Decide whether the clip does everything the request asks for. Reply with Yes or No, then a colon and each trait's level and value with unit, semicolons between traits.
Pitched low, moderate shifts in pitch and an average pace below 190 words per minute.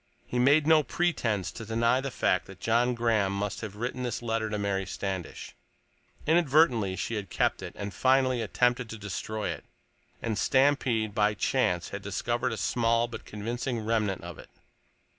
Yes: low, 115 Hz; average, 3.3 semitones; average, 170 wpm